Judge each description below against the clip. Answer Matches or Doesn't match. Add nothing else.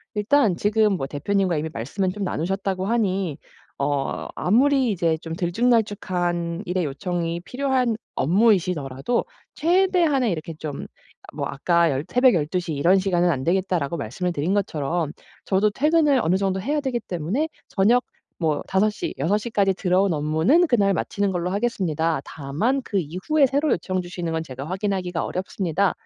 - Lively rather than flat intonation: Doesn't match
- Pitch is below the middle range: Doesn't match